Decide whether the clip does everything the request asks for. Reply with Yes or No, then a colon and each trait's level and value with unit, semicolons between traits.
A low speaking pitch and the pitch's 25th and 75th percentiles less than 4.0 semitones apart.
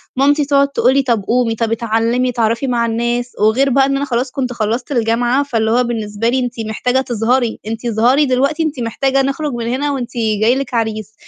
No: high, 245 Hz; average, 2.9 semitones